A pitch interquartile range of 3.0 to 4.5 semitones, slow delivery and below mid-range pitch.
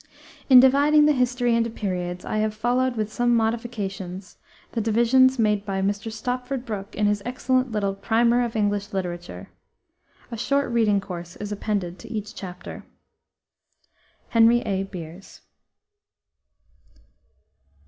No: average, 3.5 semitones; slow, 130 wpm; high, 220 Hz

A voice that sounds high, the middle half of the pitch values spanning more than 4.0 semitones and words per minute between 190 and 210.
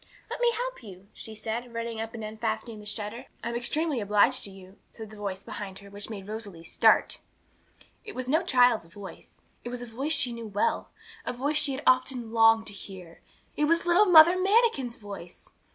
Yes: high, 230 Hz; average, 4.6 semitones; average, 200 wpm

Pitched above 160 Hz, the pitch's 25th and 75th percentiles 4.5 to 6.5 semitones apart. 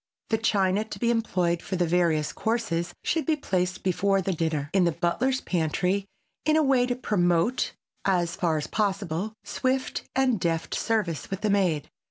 Yes: high, 190 Hz; average, 4.8 semitones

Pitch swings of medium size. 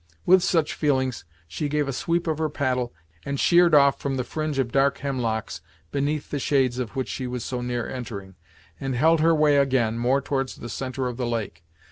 Yes: average, 3.2 semitones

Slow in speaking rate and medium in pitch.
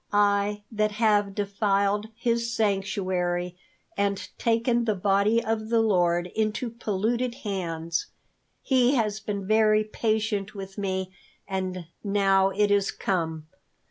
No: slow, 120 wpm; high, 205 Hz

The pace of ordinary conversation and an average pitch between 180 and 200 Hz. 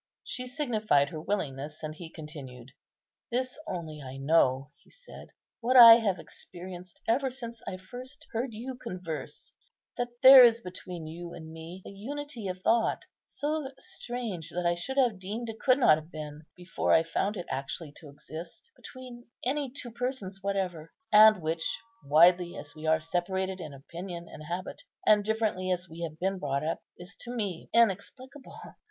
Yes: average, 170 wpm; medium, 185 Hz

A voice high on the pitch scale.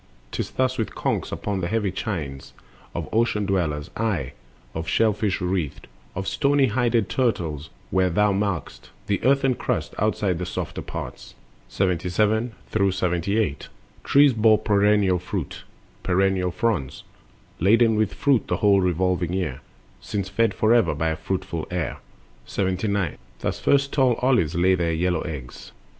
No: very low, 95 Hz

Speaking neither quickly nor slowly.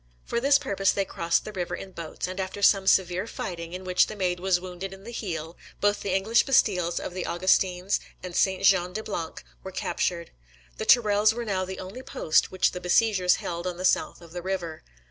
No: fast, 215 wpm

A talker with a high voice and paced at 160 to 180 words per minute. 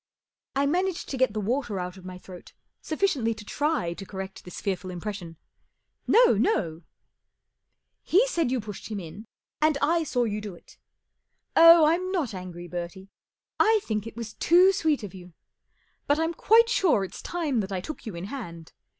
No: high, 225 Hz; average, 190 wpm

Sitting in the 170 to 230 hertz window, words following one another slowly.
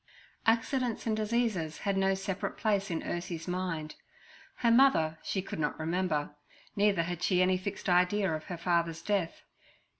No: medium, 185 Hz; average, 155 wpm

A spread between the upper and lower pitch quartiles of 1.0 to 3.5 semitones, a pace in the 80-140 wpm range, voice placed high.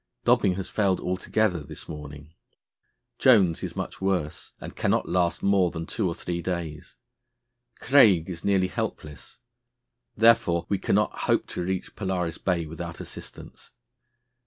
No: average, 2.8 semitones; slow, 135 wpm; very low, 90 Hz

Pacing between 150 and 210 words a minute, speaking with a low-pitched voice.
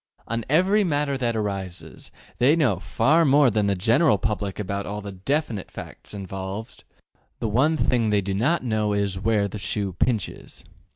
Yes: average, 170 wpm; low, 110 Hz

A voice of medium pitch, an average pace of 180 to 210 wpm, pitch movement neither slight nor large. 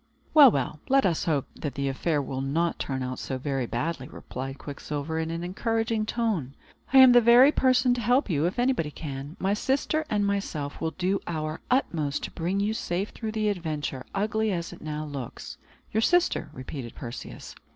No: medium, 170 Hz; average, 190 wpm; wide, 7.5 semitones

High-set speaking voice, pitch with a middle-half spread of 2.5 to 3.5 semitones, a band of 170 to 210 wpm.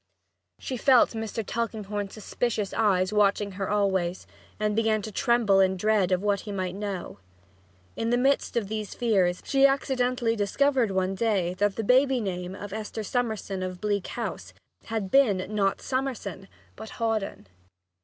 No: high, 210 Hz; average, 3.0 semitones; average, 155 wpm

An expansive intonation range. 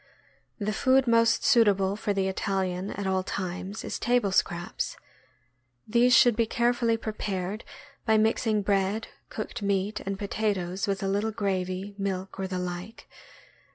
No: narrow, 2.6 semitones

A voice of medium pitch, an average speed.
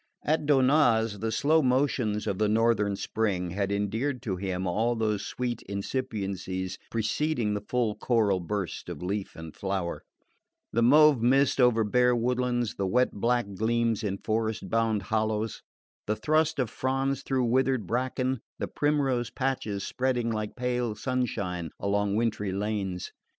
No: low, 115 Hz; average, 145 wpm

